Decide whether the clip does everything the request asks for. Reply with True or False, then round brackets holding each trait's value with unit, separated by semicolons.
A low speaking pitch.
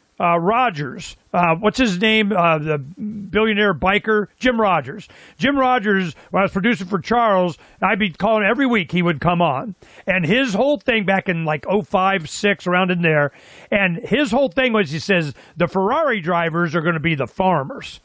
False (195 Hz)